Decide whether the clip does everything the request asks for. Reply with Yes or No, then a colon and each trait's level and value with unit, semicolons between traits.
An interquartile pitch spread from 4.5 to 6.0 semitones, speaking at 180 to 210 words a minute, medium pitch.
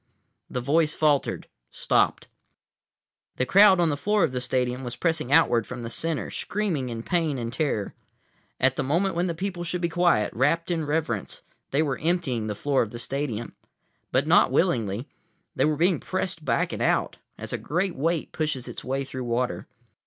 Yes: average, 5.1 semitones; average, 185 wpm; medium, 145 Hz